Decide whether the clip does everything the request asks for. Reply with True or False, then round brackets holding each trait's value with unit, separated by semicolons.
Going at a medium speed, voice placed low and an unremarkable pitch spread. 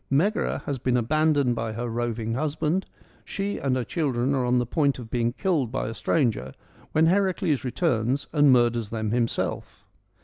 True (170 wpm; 130 Hz; 4.6 semitones)